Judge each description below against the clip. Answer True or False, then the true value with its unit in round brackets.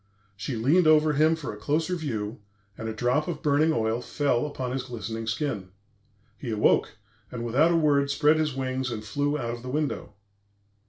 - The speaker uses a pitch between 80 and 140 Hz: True (135 Hz)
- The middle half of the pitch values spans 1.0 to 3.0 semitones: False (4.7 semitones)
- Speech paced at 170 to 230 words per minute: True (190 wpm)